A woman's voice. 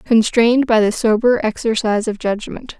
Yes: female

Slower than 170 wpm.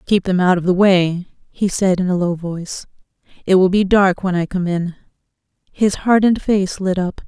No: fast, 205 wpm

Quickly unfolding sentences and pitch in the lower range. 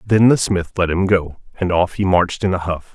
Yes: fast, 265 wpm; very low, 95 Hz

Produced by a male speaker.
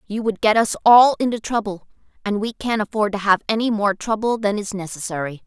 No: female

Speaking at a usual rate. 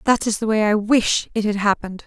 No: fast, 260 wpm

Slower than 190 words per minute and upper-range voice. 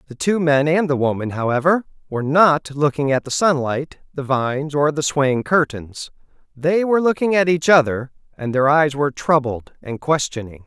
No: average, 180 wpm; medium, 145 Hz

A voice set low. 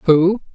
No: medium, 180 Hz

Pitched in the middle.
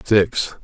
No: low, 100 Hz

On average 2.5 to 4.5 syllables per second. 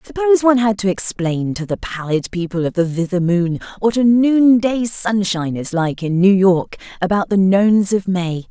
No: 5.0 syllables/s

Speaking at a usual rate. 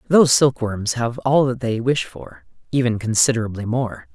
Yes: average, 145 wpm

